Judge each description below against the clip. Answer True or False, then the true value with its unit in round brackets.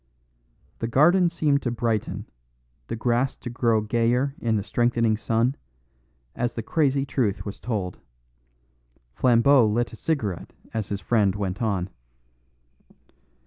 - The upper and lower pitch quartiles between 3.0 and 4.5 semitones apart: True (3.4 semitones)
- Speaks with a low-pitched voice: True (115 Hz)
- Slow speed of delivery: True (130 wpm)